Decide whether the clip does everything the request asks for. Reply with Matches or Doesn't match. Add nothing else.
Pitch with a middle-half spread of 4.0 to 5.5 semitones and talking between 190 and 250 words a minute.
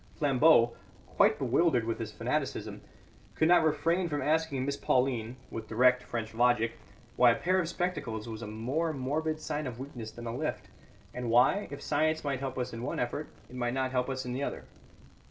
Matches